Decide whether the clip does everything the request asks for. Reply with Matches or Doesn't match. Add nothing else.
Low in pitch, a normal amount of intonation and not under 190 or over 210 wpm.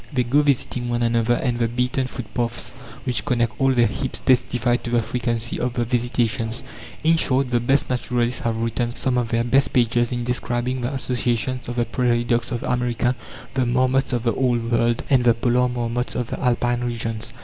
Doesn't match